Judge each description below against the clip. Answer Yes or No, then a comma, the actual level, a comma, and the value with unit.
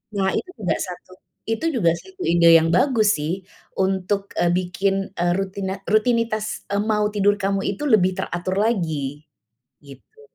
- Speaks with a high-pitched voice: Yes, high, 195 Hz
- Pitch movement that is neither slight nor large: Yes, average, 3.5 semitones